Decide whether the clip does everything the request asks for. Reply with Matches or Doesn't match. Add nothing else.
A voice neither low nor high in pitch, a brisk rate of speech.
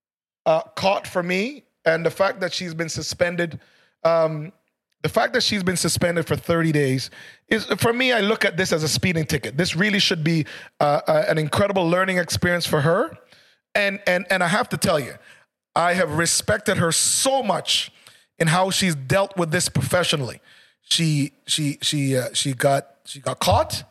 Doesn't match